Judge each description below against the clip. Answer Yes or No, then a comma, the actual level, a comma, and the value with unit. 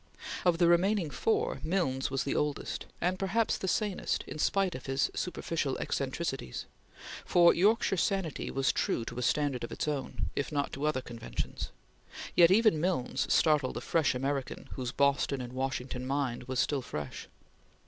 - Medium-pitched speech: Yes, medium, 145 Hz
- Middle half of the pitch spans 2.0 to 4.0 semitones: No, average, 5.3 semitones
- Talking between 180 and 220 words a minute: No, average, 165 wpm